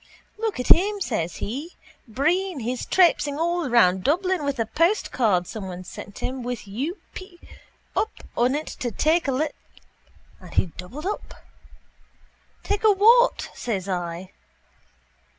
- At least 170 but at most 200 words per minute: No, average, 140 wpm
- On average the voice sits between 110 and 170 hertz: No, very high, 275 Hz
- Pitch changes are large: Yes, wide, 8.8 semitones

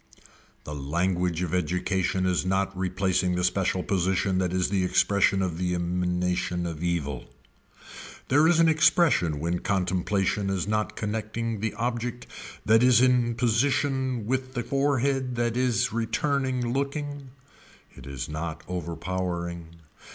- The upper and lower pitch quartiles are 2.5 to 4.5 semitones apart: No, wide, 5.5 semitones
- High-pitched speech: No, very low, 95 Hz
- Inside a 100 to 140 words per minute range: Yes, slow, 135 wpm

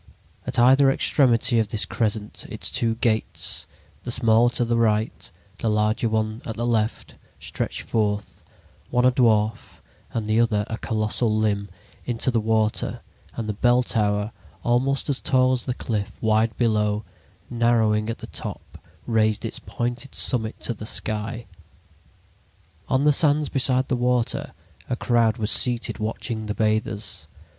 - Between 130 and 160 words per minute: Yes, average, 150 wpm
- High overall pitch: No, low, 115 Hz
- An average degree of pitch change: No, narrow, 2.2 semitones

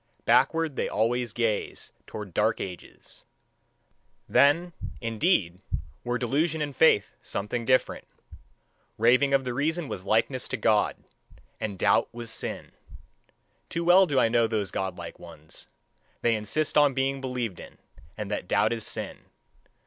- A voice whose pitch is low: Yes, low, 120 Hz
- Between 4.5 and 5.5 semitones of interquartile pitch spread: Yes, average, 4.9 semitones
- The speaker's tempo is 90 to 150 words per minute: Yes, average, 140 wpm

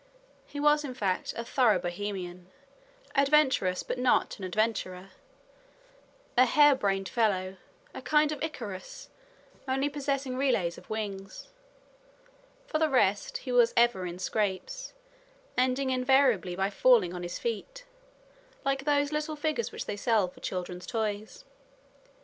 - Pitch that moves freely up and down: Yes, wide, 6.4 semitones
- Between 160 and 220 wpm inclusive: No, slow, 135 wpm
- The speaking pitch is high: Yes, high, 235 Hz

